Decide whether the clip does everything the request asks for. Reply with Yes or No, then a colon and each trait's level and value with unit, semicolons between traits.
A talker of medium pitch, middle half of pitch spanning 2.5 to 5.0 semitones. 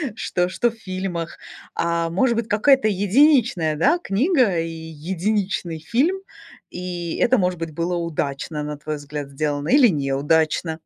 No: medium, 175 Hz; wide, 5.4 semitones